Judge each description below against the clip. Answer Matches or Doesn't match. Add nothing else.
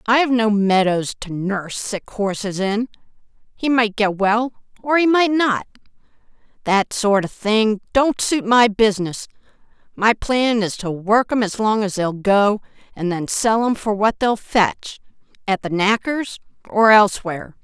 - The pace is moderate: Matches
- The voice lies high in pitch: Matches